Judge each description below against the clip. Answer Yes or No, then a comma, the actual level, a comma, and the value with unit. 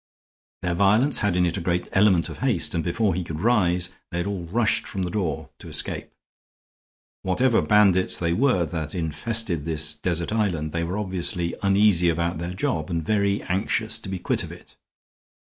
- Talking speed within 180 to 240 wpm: Yes, average, 185 wpm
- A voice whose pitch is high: No, very low, 90 Hz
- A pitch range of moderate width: Yes, average, 3.6 semitones